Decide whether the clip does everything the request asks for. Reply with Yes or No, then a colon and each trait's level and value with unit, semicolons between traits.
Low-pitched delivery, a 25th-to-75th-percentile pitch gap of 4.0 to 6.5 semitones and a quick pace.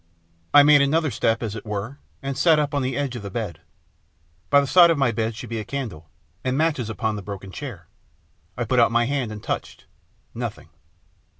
Yes: low, 125 Hz; average, 4.7 semitones; fast, 215 wpm